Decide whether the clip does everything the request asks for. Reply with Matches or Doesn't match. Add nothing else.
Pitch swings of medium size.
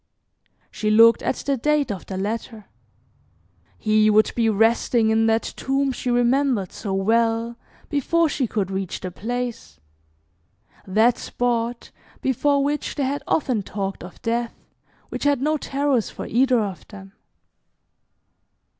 Matches